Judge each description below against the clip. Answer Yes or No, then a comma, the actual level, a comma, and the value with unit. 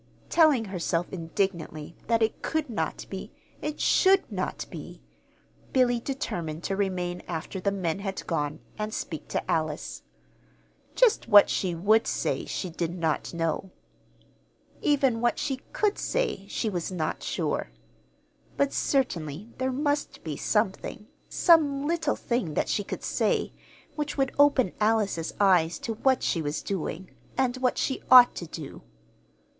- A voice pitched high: Yes, high, 205 Hz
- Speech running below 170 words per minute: Yes, average, 145 wpm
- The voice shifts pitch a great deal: Yes, wide, 7.6 semitones